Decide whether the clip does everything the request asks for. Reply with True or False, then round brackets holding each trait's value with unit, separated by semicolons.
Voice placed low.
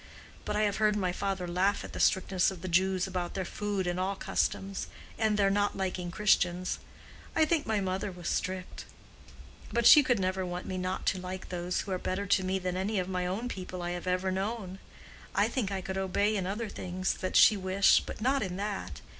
False (190 Hz)